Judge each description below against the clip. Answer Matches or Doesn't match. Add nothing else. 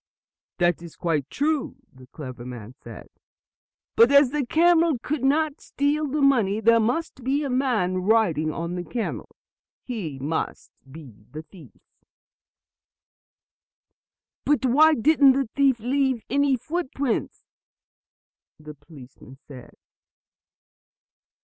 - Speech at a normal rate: Doesn't match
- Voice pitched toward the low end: Doesn't match